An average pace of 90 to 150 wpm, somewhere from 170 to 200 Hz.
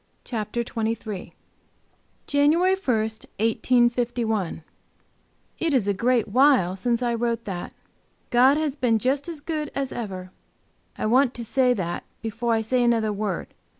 No: average, 145 wpm; high, 235 Hz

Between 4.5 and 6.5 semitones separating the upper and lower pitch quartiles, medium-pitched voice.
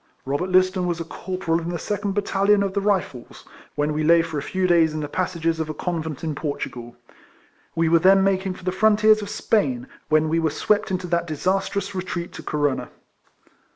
No: average, 3.5 semitones; medium, 180 Hz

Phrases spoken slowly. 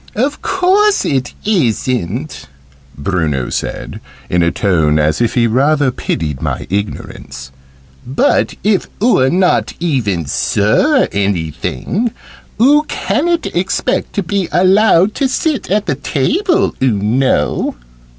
Yes: slow, 120 wpm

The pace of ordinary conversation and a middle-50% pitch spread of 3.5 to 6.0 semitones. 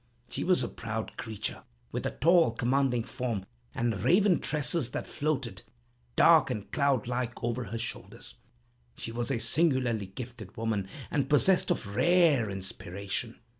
Yes: average, 145 wpm; average, 4.1 semitones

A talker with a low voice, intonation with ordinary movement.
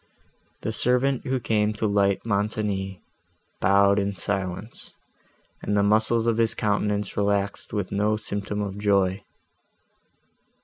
No: low, 105 Hz; narrow, 1.4 semitones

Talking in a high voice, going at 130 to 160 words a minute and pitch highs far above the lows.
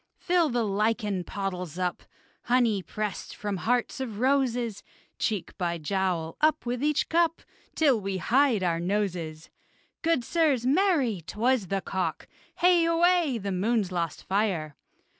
Yes: high, 215 Hz; average, 140 wpm; wide, 6.3 semitones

